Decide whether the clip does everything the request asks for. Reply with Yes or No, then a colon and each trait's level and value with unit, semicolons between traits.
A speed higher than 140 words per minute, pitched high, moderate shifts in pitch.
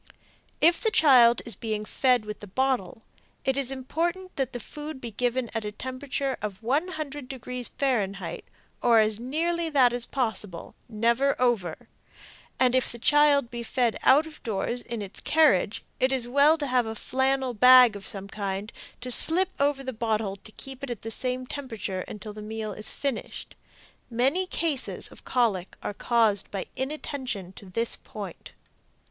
Yes: average, 170 wpm; high, 245 Hz; average, 4.0 semitones